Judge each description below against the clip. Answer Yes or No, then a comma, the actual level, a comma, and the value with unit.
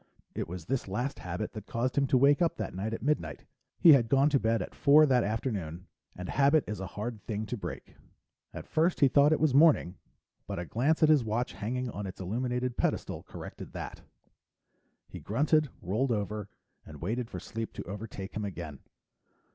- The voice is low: Yes, low, 115 Hz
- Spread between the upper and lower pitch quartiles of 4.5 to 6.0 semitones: Yes, wide, 5.5 semitones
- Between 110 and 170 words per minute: No, average, 195 wpm